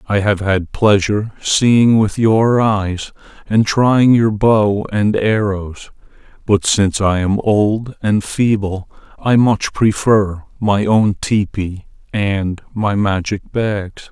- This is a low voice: Yes, low, 105 Hz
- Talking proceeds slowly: Yes, slow, 130 wpm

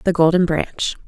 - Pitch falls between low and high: Yes, medium, 165 Hz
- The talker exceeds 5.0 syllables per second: No, 4.7 syllables/s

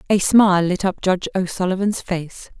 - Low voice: No, medium, 185 Hz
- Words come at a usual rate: Yes, average, 160 wpm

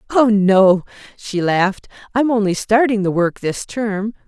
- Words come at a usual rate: No, slow, 125 wpm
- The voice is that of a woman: Yes, female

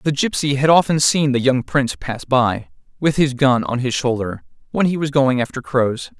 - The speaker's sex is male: Yes, male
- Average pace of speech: No, fast, 215 wpm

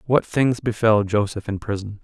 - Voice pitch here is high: No, low, 110 Hz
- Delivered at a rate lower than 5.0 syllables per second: Yes, 4.8 syllables/s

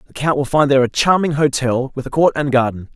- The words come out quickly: Yes, fast, 265 wpm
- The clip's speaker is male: Yes, male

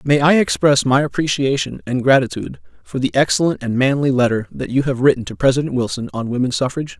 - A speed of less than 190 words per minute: No, average, 195 wpm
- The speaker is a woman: No, male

